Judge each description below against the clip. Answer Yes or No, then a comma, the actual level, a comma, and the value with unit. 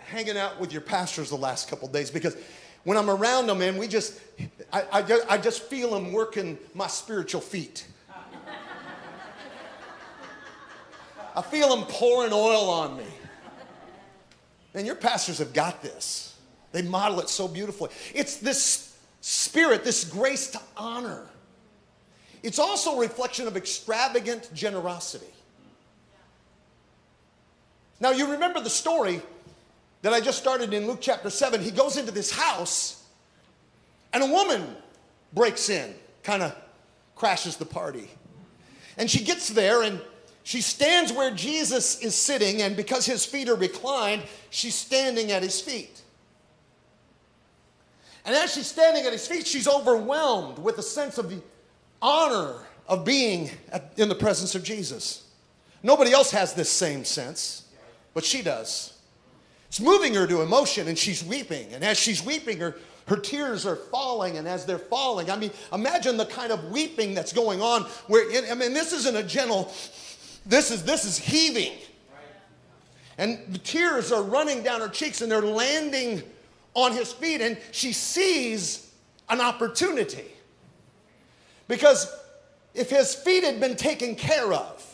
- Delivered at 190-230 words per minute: No, average, 150 wpm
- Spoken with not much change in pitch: No, average, 5.3 semitones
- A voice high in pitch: Yes, high, 235 Hz